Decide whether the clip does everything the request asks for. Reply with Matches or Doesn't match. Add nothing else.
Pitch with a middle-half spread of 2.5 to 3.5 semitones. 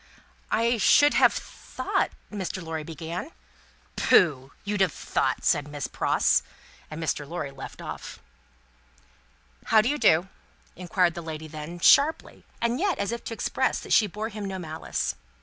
Doesn't match